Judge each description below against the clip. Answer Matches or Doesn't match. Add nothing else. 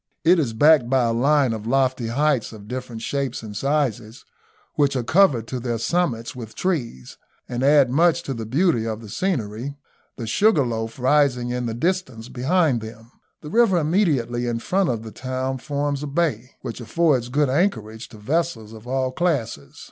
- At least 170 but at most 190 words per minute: Matches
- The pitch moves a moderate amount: Matches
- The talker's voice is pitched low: Matches